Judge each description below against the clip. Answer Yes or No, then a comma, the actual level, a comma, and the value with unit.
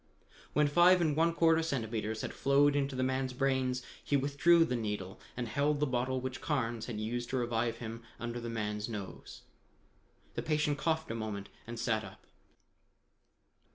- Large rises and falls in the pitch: No, average, 4.1 semitones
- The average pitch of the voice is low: Yes, low, 130 Hz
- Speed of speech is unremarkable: Yes, average, 170 wpm